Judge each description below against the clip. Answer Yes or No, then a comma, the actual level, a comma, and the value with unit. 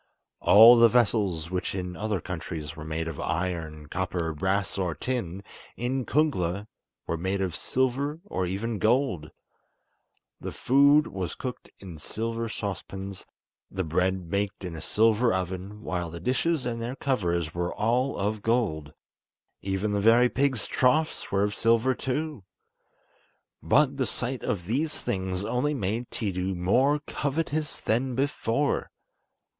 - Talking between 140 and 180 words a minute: Yes, average, 145 wpm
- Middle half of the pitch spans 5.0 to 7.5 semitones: Yes, wide, 5.6 semitones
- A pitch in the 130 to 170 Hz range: No, low, 105 Hz